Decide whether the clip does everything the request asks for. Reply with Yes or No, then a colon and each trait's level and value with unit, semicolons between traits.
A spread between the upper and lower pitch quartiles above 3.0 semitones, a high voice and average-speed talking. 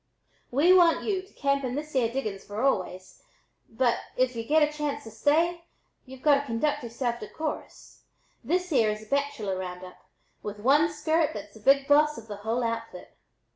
Yes: average, 5.3 semitones; very high, 260 Hz; average, 190 wpm